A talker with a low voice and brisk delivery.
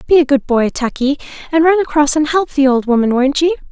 No: very high, 290 Hz; fast, 245 wpm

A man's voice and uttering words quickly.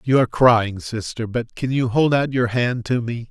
Yes: male; fast, 235 wpm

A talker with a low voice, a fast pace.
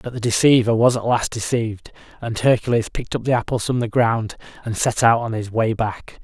Yes: low, 115 Hz; fast, 220 wpm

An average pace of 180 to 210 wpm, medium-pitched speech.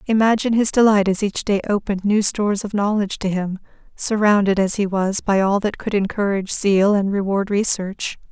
No: average, 190 wpm; high, 200 Hz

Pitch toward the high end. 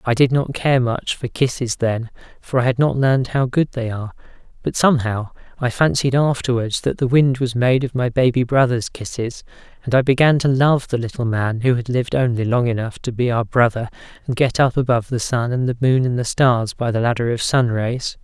No: low, 125 Hz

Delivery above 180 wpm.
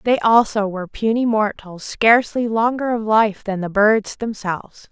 No: average, 160 wpm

